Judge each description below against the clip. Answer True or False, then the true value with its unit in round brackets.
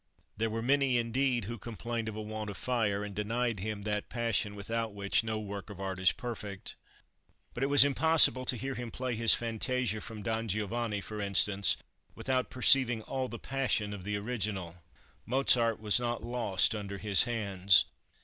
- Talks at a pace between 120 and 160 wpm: False (180 wpm)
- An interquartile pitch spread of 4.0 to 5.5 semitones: False (3.0 semitones)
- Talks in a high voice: False (110 Hz)